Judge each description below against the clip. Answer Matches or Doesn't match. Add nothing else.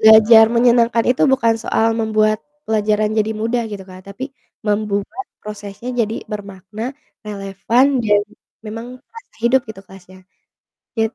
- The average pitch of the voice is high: Matches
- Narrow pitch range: Matches